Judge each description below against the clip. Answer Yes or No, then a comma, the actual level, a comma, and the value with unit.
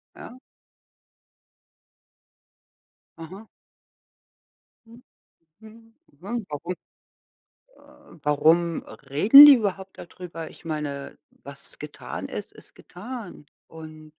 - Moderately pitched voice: Yes, medium, 180 Hz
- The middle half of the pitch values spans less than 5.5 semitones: No, wide, 6.1 semitones